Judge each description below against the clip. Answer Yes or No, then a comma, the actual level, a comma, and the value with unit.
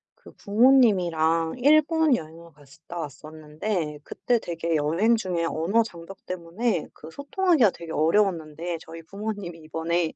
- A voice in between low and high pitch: Yes, medium, 170 Hz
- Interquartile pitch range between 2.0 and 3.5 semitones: No, average, 5.2 semitones